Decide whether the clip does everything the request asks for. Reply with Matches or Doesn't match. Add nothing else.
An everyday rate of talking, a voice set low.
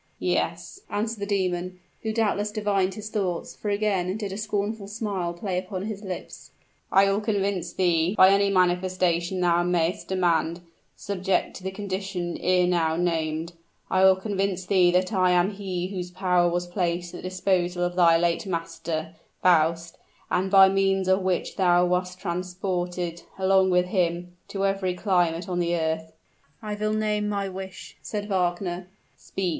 Doesn't match